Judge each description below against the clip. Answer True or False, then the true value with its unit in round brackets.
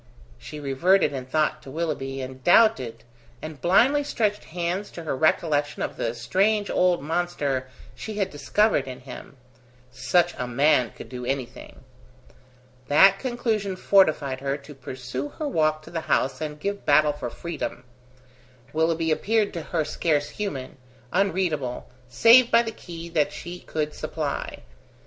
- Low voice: False (155 Hz)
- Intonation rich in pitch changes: True (5.7 semitones)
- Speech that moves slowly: False (150 wpm)